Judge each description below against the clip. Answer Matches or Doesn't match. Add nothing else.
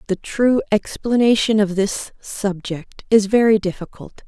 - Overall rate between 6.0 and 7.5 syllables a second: Doesn't match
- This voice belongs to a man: Doesn't match